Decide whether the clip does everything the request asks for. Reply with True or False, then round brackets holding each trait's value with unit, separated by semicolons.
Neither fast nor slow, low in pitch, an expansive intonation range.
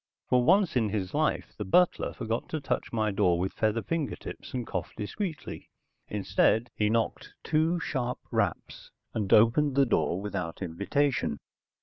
True (150 wpm; 115 Hz; 6.0 semitones)